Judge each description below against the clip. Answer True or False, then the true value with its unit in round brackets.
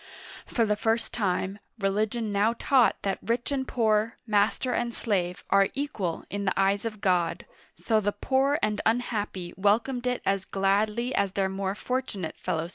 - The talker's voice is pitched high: True (210 Hz)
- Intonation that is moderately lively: True (3.3 semitones)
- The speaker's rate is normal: True (170 wpm)